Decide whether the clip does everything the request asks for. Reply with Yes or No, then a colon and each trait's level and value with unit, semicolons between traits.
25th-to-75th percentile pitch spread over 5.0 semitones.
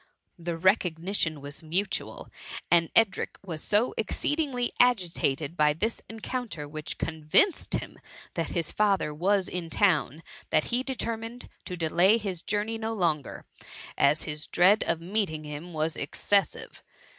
Yes: wide, 5.5 semitones